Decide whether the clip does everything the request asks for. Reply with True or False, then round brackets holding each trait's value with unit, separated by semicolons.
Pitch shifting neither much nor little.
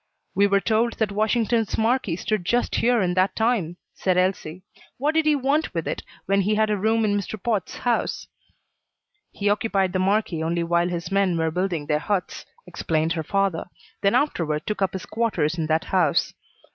True (4.2 semitones)